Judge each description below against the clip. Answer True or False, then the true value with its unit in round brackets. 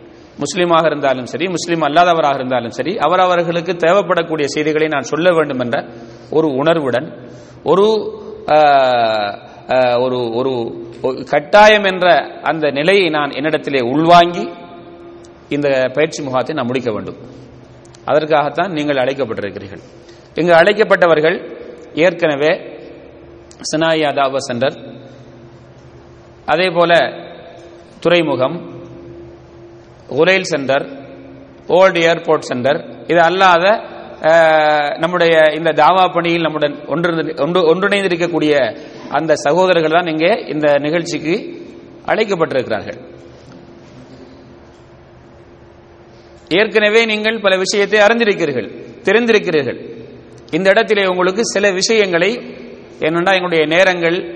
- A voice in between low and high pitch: True (160 Hz)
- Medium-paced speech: False (85 wpm)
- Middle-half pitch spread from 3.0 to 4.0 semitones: False (4.5 semitones)